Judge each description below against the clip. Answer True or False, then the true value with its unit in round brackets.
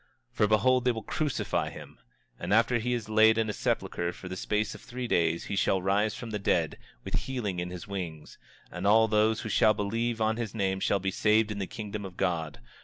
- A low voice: True (105 Hz)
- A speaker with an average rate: False (225 wpm)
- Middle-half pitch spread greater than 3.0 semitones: False (2.7 semitones)